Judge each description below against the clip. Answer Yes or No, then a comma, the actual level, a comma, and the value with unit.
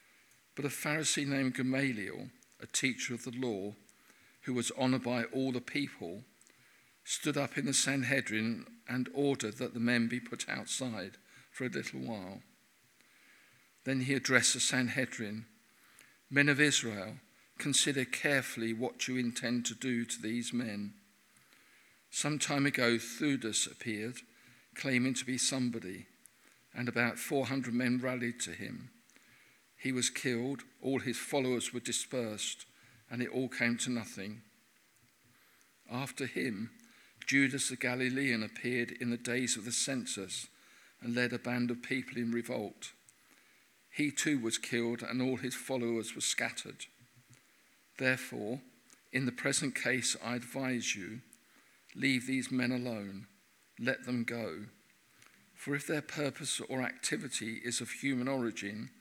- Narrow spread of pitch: Yes, narrow, 2.0 semitones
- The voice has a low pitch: Yes, low, 125 Hz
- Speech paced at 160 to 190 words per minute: No, average, 140 wpm